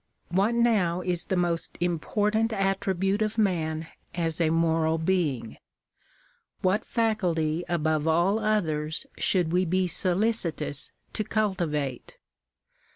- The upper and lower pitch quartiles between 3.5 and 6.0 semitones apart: Yes, average, 4.1 semitones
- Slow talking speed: Yes, slow, 110 wpm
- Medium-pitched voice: Yes, medium, 175 Hz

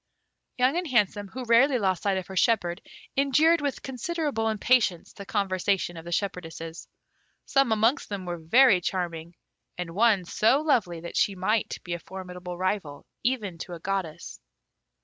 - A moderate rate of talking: Yes, average, 160 wpm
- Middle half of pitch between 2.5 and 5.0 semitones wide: No, wide, 5.6 semitones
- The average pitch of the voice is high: Yes, high, 200 Hz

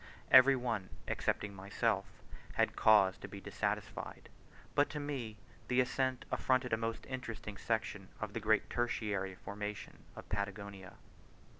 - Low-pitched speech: Yes, low, 110 Hz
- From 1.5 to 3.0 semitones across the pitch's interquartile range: No, average, 3.7 semitones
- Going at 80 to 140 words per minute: Yes, slow, 135 wpm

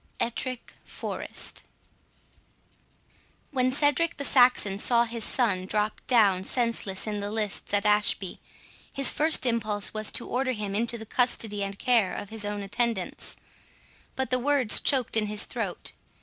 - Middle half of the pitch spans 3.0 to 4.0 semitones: Yes, average, 3.5 semitones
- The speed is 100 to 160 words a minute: Yes, average, 150 wpm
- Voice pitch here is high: Yes, high, 225 Hz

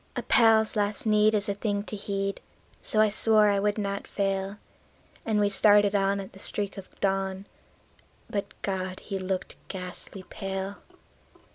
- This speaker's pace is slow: No, average, 160 wpm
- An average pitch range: No, narrow, 1.3 semitones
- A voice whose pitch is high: Yes, high, 200 Hz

